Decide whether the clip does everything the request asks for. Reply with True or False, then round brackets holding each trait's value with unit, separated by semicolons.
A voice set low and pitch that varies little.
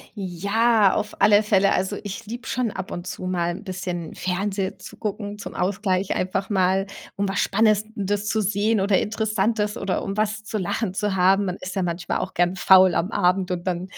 False (195 Hz; 2.3 semitones)